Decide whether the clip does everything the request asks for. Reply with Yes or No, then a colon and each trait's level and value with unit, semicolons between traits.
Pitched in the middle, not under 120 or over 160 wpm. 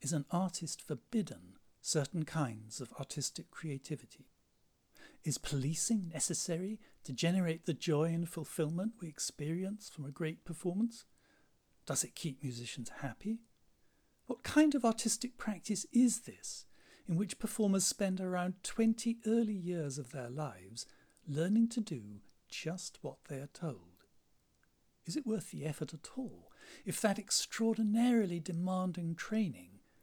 Yes: medium, 170 Hz; slow, 135 wpm